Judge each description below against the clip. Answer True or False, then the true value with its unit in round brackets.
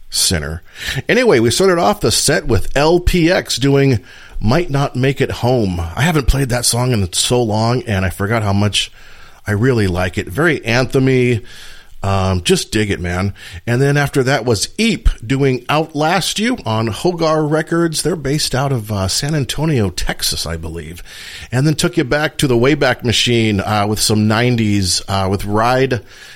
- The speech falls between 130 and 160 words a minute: False (175 wpm)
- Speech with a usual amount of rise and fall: False (6.1 semitones)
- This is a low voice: True (120 Hz)